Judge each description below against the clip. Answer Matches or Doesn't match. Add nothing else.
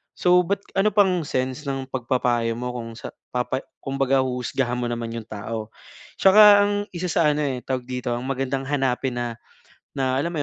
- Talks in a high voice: Doesn't match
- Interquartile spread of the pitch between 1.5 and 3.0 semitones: Doesn't match